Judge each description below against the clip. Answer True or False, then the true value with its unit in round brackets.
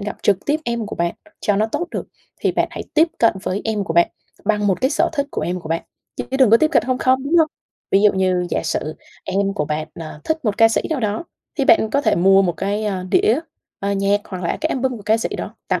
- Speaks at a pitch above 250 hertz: False (210 Hz)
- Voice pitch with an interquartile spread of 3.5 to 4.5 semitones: False (5.2 semitones)